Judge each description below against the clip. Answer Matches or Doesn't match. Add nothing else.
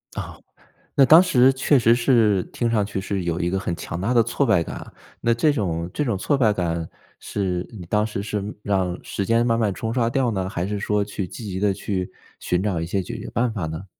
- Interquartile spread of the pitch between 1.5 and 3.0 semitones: Doesn't match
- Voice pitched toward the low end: Matches